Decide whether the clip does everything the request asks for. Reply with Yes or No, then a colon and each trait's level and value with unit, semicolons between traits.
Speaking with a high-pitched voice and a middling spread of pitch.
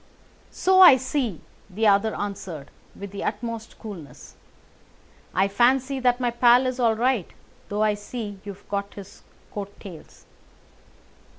Yes: high, 215 Hz; average, 3.6 semitones